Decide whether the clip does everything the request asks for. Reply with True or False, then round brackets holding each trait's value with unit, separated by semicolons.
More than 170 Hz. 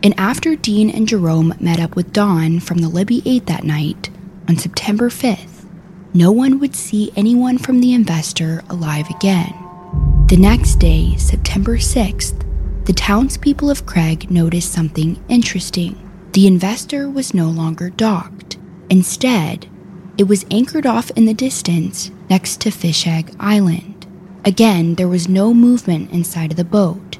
True (185 Hz)